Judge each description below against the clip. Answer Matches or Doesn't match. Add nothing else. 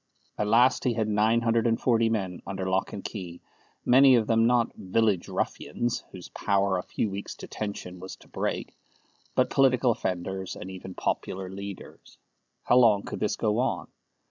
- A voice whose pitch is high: Doesn't match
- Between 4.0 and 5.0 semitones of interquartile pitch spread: Doesn't match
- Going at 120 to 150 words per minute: Doesn't match